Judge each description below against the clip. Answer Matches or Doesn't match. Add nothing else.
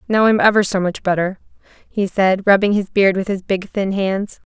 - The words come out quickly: Matches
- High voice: Matches